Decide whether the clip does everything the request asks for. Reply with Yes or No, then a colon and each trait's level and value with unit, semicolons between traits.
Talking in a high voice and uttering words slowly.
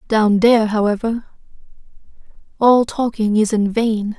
Yes: high, 220 Hz; slow, 100 wpm